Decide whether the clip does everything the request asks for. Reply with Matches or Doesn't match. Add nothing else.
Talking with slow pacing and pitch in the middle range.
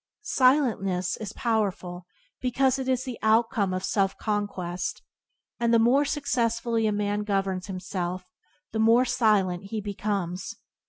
Doesn't match